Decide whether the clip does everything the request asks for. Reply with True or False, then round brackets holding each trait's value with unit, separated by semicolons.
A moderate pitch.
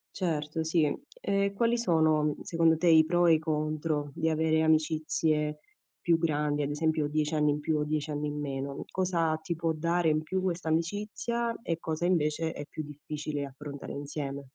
True (155 Hz)